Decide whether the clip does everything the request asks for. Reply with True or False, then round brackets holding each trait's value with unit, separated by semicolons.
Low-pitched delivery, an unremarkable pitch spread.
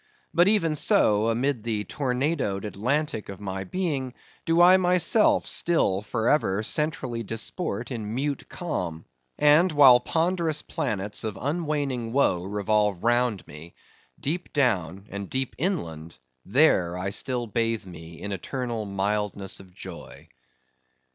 False (115 Hz; 7.0 semitones)